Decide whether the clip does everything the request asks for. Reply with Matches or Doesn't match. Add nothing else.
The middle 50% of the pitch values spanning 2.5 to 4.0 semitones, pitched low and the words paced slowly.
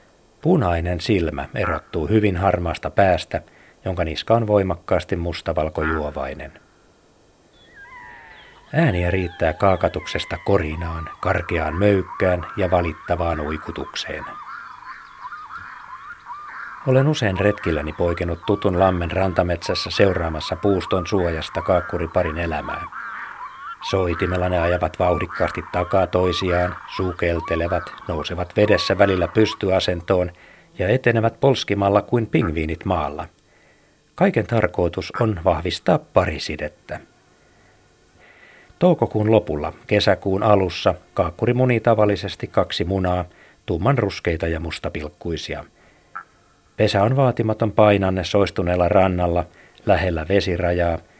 Matches